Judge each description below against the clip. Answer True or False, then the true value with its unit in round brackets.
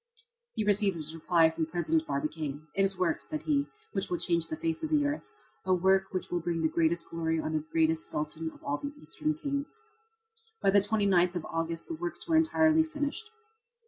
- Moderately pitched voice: True (175 Hz)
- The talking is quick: True (210 wpm)